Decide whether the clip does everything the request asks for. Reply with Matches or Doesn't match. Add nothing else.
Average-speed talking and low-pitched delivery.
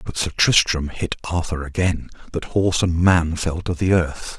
Matches